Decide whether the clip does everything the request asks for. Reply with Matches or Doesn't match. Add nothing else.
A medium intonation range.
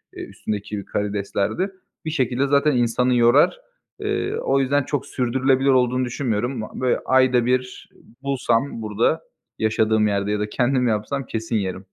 Matches